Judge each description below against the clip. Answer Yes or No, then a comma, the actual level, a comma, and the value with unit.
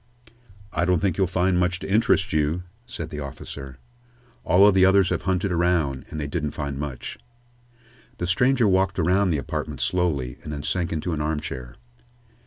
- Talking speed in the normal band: Yes, average, 180 wpm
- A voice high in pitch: No, very low, 85 Hz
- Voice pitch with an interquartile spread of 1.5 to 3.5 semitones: No, average, 4.0 semitones